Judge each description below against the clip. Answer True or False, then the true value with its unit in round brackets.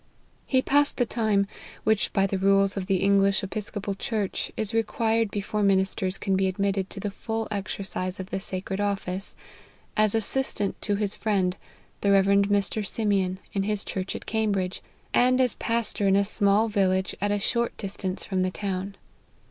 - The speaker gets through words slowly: False (175 wpm)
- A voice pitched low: False (200 Hz)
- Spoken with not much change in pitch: True (1.8 semitones)